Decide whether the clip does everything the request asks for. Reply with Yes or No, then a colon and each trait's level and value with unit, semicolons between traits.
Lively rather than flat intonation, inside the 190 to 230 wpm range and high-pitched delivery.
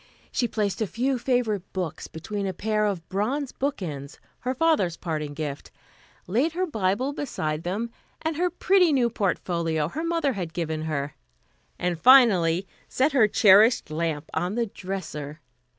No: wide, 7.5 semitones; average, 150 wpm; high, 200 Hz